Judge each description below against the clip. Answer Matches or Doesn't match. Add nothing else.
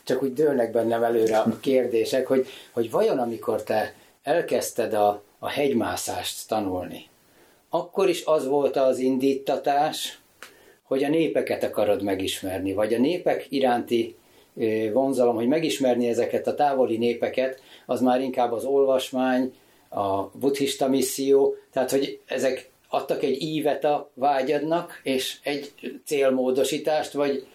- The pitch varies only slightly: Doesn't match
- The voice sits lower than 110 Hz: Doesn't match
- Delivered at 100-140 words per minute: Matches